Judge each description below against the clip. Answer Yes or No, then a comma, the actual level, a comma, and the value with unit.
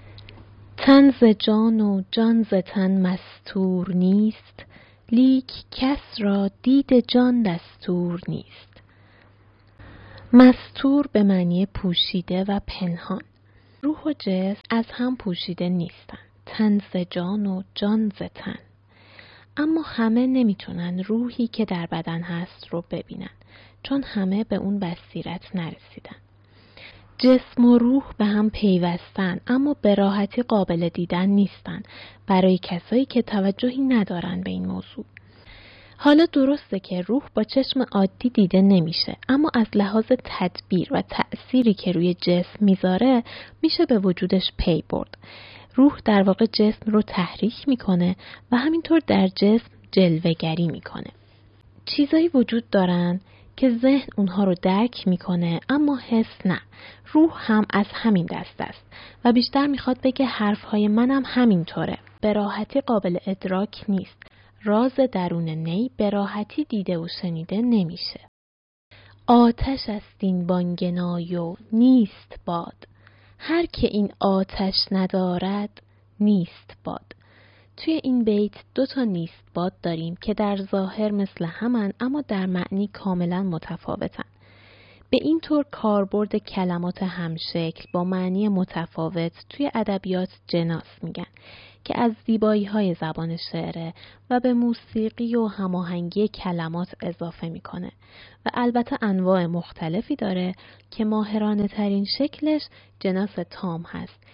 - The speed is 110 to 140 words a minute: Yes, average, 125 wpm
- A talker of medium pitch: No, high, 195 Hz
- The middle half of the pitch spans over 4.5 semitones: Yes, average, 4.9 semitones